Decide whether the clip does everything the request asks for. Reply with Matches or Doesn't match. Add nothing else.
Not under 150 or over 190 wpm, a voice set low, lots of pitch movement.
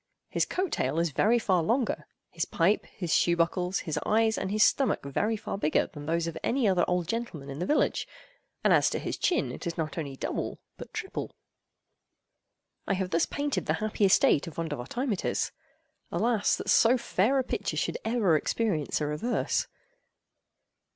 Doesn't match